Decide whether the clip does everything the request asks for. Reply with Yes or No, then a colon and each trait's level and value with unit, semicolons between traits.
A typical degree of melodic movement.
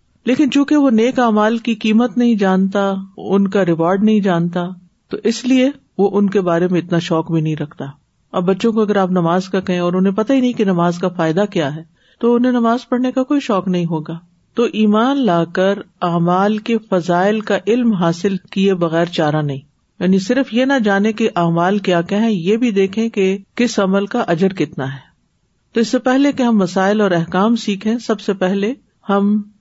Yes: average, 4.3 semitones